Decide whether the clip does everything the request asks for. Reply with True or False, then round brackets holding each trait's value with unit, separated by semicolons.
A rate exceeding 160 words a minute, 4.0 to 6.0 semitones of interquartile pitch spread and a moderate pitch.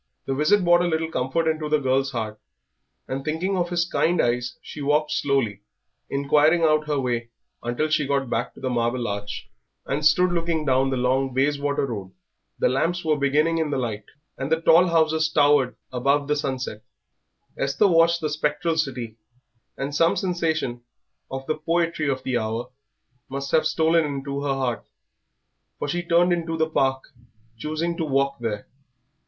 False (170 wpm; 3.6 semitones; 145 Hz)